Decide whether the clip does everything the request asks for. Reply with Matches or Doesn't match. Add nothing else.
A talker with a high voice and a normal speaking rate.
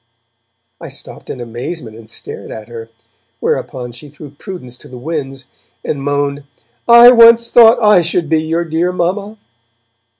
Doesn't match